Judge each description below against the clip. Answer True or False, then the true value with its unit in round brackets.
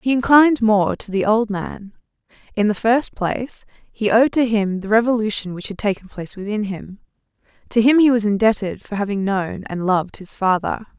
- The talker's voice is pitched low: False (215 Hz)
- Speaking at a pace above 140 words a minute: True (190 wpm)